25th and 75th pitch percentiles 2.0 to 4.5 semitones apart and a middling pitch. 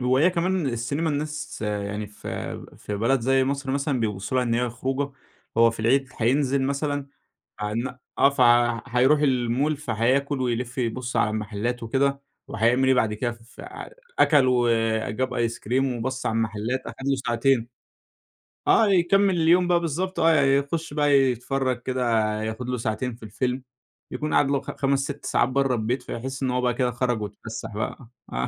No: average, 3.1 semitones; low, 130 Hz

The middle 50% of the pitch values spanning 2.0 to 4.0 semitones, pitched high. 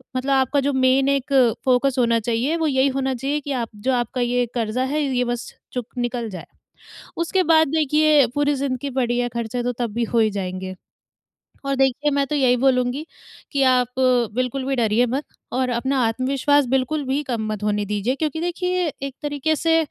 Yes: average, 2.8 semitones; very high, 260 Hz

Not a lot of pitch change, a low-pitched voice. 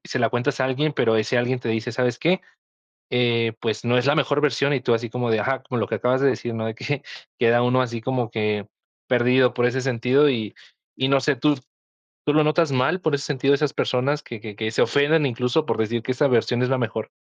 No: average, 3.0 semitones; low, 125 Hz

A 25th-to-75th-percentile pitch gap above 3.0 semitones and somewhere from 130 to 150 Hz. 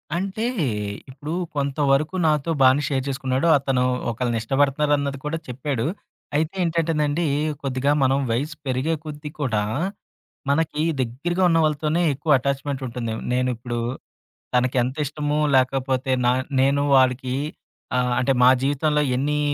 No: average, 2.7 semitones; medium, 140 Hz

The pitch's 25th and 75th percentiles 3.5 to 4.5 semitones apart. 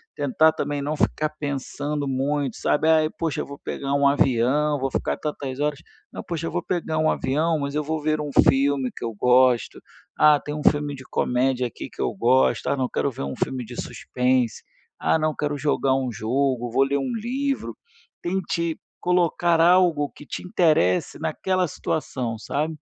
No: average, 3.1 semitones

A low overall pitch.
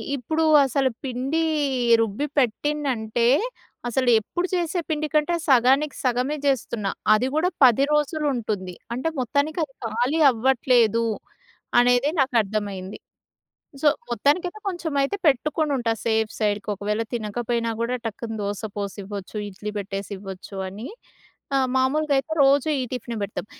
No: high, 245 Hz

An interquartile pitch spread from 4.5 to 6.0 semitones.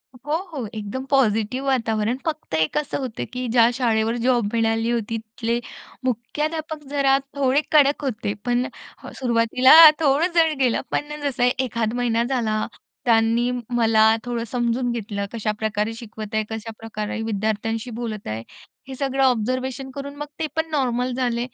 No: average, 3.2 semitones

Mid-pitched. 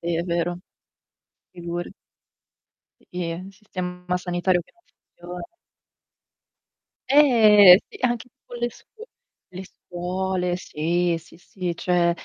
Yes: medium, 180 Hz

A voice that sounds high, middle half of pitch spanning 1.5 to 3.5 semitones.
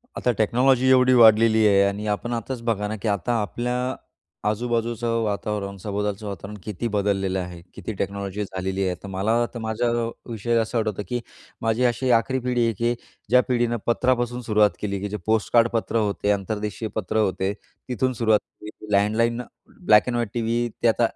No: low, 110 Hz; narrow, 2.6 semitones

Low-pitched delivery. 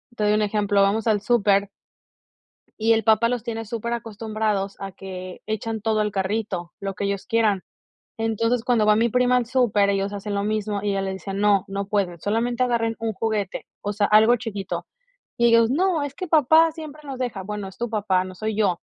No: high, 215 Hz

